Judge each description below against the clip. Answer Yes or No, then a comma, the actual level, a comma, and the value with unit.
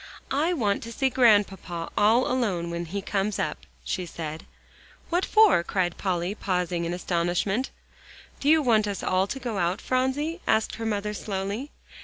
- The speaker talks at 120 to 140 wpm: No, average, 165 wpm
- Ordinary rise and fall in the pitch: No, wide, 5.9 semitones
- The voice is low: No, high, 205 Hz